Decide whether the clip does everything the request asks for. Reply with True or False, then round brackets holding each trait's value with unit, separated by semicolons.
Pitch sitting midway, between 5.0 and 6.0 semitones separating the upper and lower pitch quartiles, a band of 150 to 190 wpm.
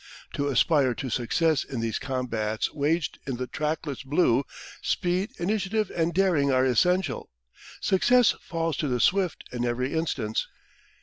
False (145 Hz; 5.5 semitones; 140 wpm)